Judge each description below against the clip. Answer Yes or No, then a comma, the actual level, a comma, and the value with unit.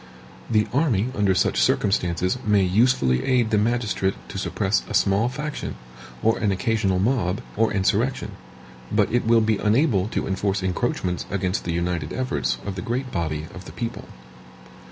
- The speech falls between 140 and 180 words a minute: Yes, average, 160 wpm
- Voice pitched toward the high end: No, low, 100 Hz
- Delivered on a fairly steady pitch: No, average, 4.0 semitones